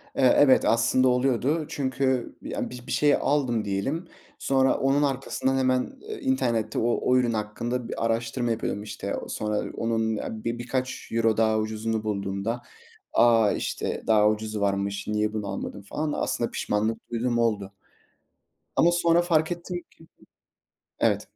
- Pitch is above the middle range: No, low, 115 Hz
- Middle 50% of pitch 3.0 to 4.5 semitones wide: Yes, average, 3.7 semitones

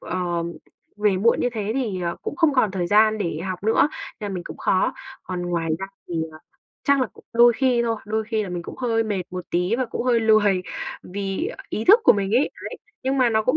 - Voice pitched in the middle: No, high, 215 Hz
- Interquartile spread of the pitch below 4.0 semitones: No, average, 4.3 semitones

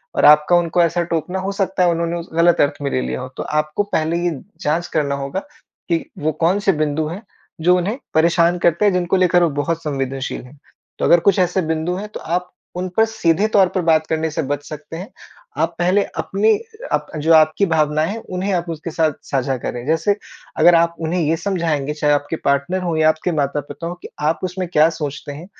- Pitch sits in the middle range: Yes, medium, 165 Hz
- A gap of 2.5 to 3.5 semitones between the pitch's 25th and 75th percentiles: Yes, average, 2.9 semitones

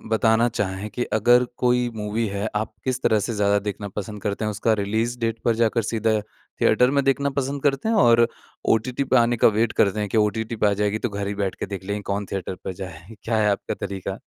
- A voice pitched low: Yes, low, 110 Hz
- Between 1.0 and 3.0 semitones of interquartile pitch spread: Yes, narrow, 2.6 semitones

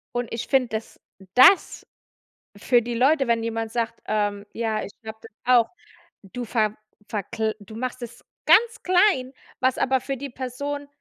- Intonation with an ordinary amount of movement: Yes, average, 3.0 semitones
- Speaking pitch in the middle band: No, high, 240 Hz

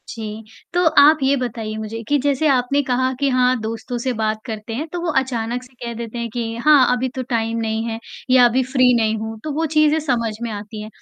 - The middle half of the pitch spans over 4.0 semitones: No, average, 2.9 semitones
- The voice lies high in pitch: Yes, high, 245 Hz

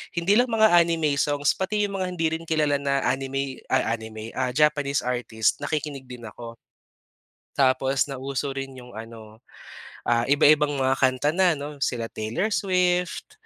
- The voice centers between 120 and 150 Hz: Yes, medium, 140 Hz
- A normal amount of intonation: Yes, average, 4.5 semitones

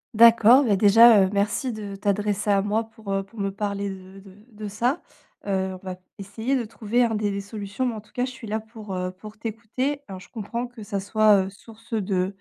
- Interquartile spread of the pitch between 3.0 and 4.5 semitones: No, narrow, 2.5 semitones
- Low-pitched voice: No, high, 210 Hz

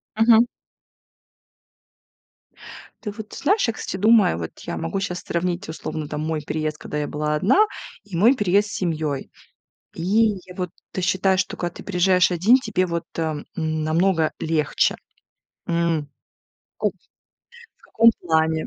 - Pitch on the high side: No, medium, 175 Hz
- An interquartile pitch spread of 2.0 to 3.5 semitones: No, average, 4.3 semitones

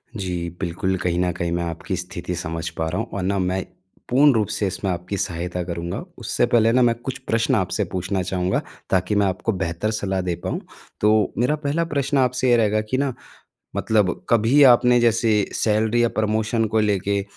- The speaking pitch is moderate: No, low, 100 Hz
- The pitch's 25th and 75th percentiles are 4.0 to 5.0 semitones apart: Yes, average, 4.3 semitones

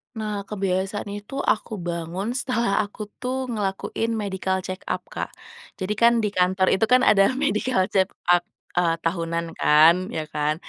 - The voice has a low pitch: No, high, 195 Hz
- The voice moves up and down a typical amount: Yes, average, 3.1 semitones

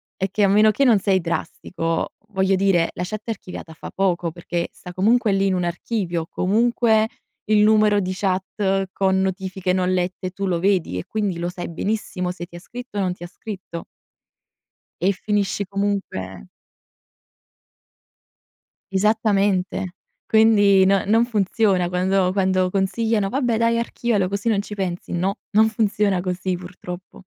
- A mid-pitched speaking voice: No, high, 195 Hz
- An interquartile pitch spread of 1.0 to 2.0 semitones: No, narrow, 2.6 semitones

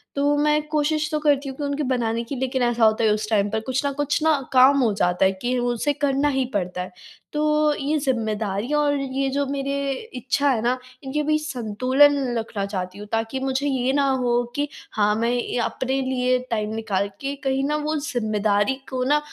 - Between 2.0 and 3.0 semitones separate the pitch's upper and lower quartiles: No, average, 4.2 semitones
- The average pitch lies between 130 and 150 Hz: No, very high, 260 Hz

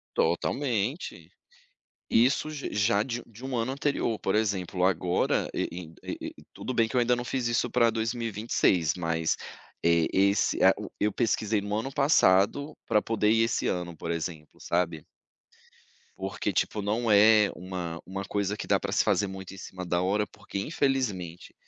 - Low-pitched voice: Yes, low, 105 Hz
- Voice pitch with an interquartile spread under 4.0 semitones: No, average, 4.4 semitones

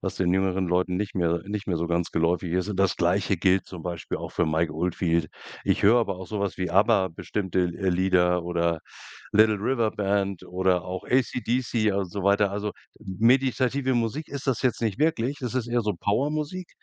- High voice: No, low, 100 Hz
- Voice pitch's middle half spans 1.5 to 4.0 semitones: No, average, 4.4 semitones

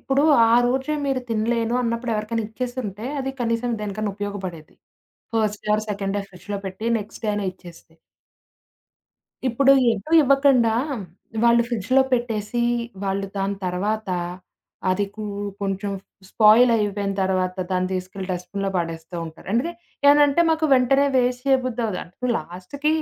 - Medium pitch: No, high, 215 Hz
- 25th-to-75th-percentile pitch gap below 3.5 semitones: No, average, 4.2 semitones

